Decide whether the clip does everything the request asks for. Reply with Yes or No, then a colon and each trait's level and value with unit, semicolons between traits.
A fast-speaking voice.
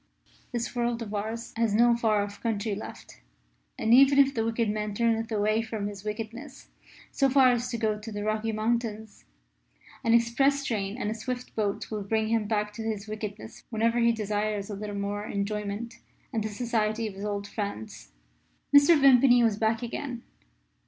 No: average, 180 wpm